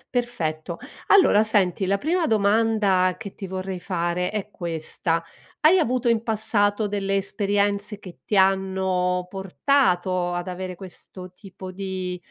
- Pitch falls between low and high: No, high, 195 Hz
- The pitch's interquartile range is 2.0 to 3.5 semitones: Yes, narrow, 2.5 semitones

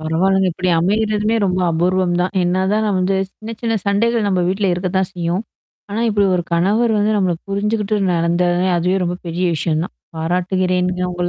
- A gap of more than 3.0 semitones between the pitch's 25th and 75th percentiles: No, narrow, 2.6 semitones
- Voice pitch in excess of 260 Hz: No, medium, 185 Hz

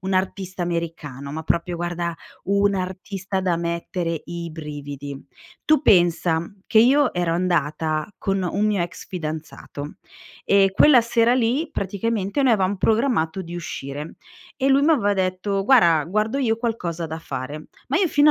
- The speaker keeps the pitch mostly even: No, average, 4.6 semitones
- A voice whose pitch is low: No, medium, 185 Hz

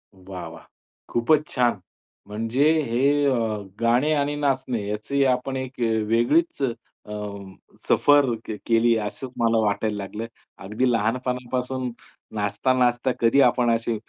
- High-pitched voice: No, low, 120 Hz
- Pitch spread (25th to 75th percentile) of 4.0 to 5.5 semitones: No, average, 2.9 semitones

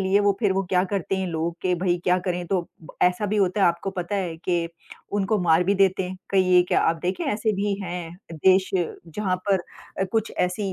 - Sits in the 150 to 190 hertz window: Yes, medium, 185 Hz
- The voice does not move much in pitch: Yes, narrow, 1.8 semitones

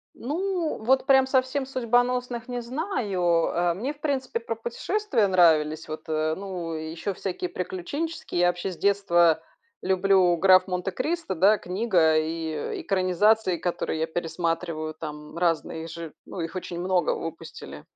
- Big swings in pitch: Yes, wide, 6.3 semitones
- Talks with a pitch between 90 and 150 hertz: No, medium, 185 Hz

